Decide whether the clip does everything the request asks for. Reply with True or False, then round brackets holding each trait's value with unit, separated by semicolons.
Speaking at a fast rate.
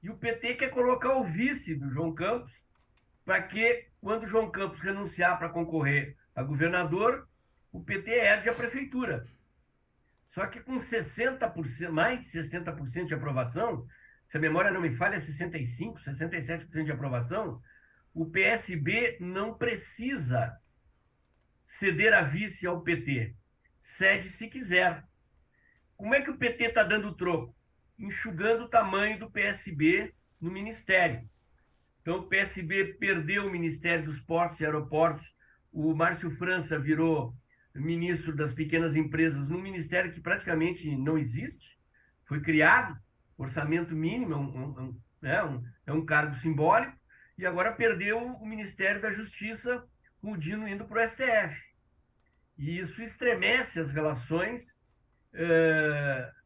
False (135 wpm)